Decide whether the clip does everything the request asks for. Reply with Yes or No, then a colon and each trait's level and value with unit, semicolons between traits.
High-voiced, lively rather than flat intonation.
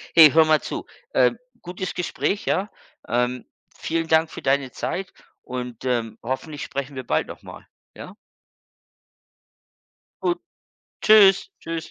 No: medium, 155 Hz; wide, 5.8 semitones